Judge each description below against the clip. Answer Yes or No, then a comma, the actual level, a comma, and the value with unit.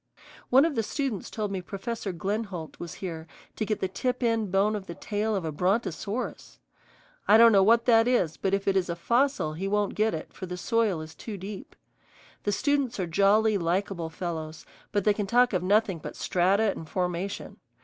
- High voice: Yes, high, 200 Hz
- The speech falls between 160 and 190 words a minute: No, average, 200 wpm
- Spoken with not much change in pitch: No, average, 3.7 semitones